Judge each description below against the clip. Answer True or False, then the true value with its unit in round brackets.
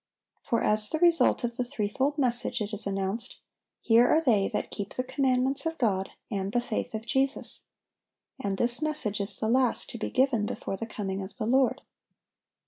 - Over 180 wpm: True (190 wpm)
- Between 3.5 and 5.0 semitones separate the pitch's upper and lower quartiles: True (4.0 semitones)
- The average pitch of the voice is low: False (235 Hz)